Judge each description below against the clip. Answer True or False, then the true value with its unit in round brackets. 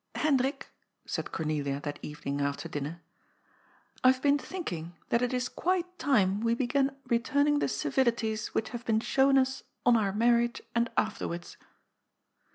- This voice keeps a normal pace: True (165 wpm)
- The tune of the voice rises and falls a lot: True (6.5 semitones)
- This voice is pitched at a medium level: False (235 Hz)